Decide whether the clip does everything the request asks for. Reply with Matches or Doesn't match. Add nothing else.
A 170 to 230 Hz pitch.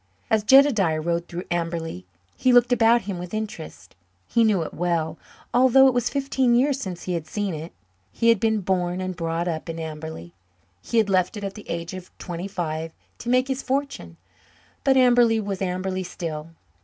Matches